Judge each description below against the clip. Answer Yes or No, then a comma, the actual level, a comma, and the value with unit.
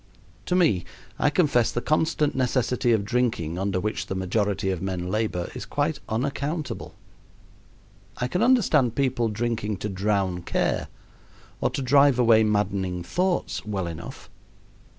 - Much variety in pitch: Yes, wide, 6.0 semitones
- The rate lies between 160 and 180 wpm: No, average, 140 wpm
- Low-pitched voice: Yes, low, 110 Hz